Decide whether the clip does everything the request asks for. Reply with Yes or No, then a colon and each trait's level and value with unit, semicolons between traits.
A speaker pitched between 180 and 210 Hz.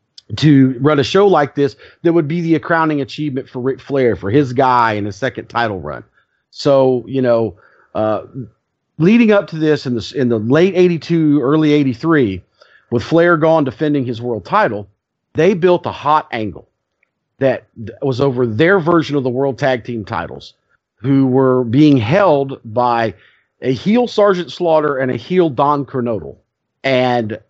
No: low, 135 Hz